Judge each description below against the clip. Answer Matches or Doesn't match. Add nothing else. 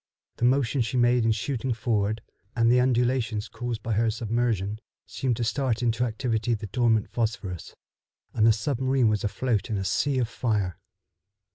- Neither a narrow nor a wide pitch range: Doesn't match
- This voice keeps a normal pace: Matches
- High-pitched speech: Doesn't match